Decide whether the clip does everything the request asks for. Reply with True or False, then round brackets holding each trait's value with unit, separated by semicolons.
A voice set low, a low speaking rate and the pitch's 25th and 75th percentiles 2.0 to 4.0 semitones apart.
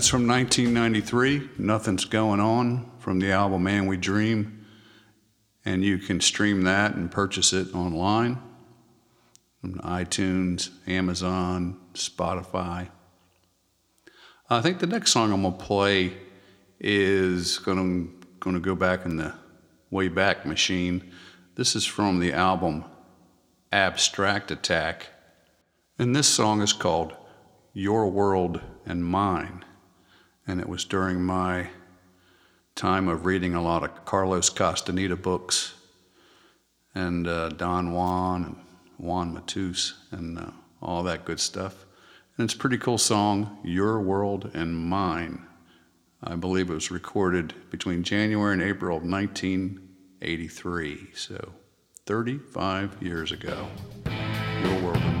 True (95 Hz; 125 wpm; 2.6 semitones)